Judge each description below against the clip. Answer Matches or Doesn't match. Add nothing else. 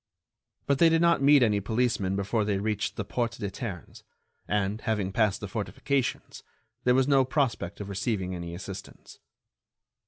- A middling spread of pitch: Matches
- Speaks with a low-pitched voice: Matches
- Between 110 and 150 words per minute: Doesn't match